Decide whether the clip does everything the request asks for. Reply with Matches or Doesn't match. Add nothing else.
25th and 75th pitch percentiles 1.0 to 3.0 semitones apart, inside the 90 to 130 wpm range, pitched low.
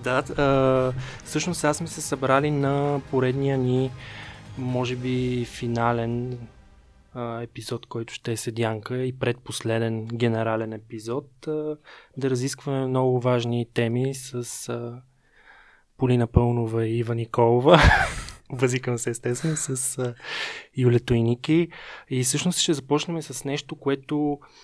Matches